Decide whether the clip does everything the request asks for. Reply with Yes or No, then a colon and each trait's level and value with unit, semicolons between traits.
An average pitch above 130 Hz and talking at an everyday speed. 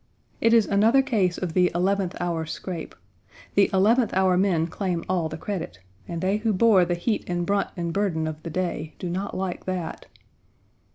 Yes: medium, 185 Hz; average, 185 wpm